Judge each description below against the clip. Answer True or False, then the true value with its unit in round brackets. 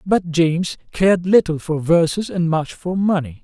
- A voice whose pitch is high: False (175 Hz)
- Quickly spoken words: False (175 wpm)